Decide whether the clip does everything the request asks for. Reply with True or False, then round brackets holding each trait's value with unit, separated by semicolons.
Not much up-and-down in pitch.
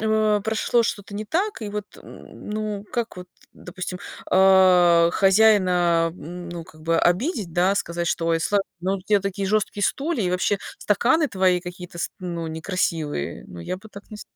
False (3.3 semitones)